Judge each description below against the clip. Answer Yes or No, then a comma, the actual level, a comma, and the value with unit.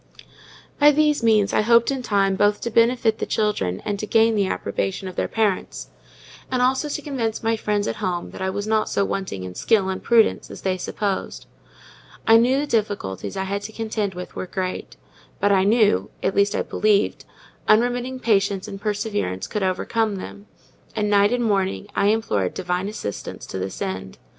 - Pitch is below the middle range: No, high, 205 Hz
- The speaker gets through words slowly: No, average, 190 wpm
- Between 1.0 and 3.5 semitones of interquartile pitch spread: Yes, average, 2.9 semitones